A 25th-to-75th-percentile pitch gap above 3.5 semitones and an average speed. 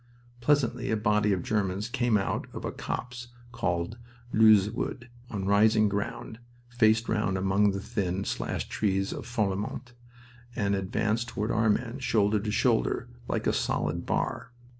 No: average, 2.9 semitones; average, 150 wpm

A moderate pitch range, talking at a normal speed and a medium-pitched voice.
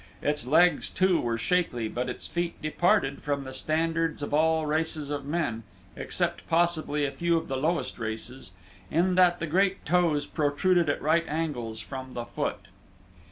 Yes: average, 3.9 semitones; average, 165 wpm; medium, 155 Hz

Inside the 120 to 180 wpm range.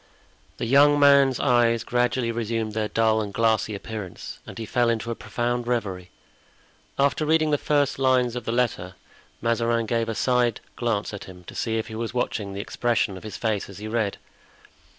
No: average, 190 wpm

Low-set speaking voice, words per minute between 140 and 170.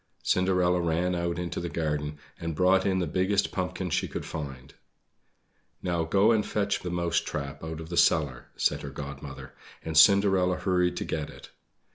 No: very low, 85 Hz; average, 180 wpm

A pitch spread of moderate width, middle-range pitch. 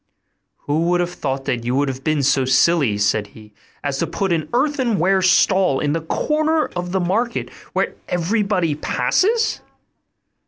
No: wide, 6.2 semitones; medium, 170 Hz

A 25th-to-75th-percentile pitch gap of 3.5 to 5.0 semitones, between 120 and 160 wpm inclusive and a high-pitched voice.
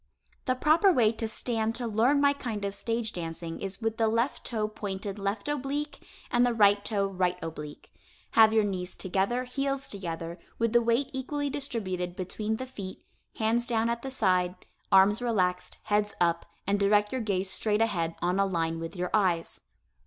No: average, 4.2 semitones; average, 180 wpm; high, 215 Hz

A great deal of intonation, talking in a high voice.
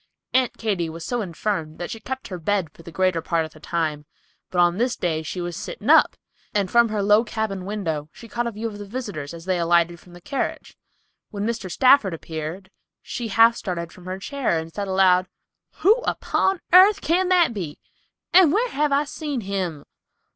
Yes: wide, 5.7 semitones; high, 195 Hz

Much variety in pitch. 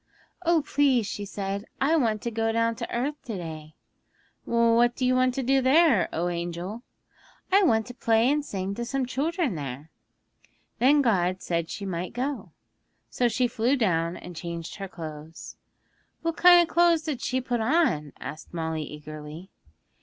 Yes: wide, 7.5 semitones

